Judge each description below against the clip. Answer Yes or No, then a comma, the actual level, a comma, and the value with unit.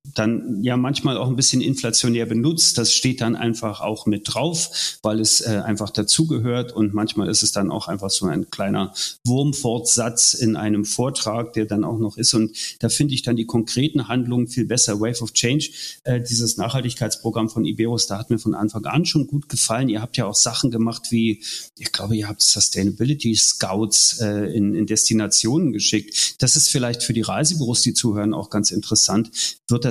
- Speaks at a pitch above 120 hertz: No, low, 115 Hz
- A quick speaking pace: Yes, fast, 195 wpm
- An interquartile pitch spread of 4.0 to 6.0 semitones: No, average, 2.7 semitones